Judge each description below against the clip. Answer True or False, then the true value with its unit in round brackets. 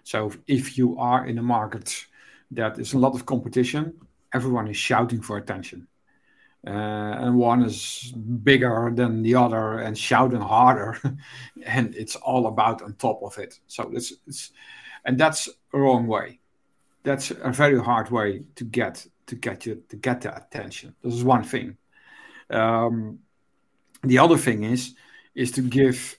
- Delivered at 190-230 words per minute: False (165 wpm)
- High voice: False (125 Hz)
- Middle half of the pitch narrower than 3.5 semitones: True (2.5 semitones)